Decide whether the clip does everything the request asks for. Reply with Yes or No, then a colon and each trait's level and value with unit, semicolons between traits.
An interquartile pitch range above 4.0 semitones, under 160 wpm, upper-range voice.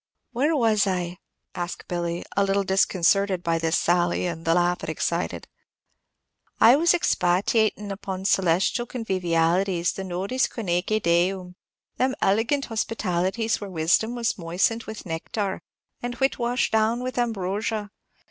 Yes: average, 4.4 semitones; slow, 135 wpm; high, 195 Hz